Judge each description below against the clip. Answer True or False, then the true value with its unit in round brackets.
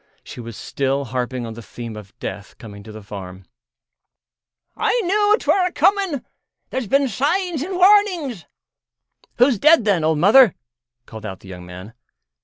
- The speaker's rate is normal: True (160 wpm)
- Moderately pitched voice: True (170 Hz)